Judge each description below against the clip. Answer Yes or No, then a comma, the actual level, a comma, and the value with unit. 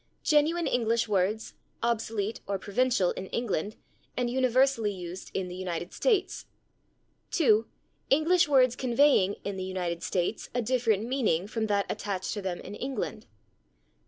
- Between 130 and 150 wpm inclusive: Yes, average, 140 wpm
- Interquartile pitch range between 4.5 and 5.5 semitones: Yes, average, 5.1 semitones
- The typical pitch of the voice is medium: No, high, 220 Hz